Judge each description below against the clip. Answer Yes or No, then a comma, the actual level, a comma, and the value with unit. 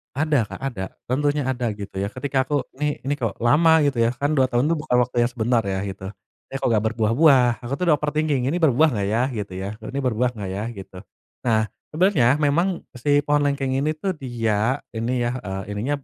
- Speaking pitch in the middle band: No, low, 125 Hz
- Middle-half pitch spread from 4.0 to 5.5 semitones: Yes, average, 4.4 semitones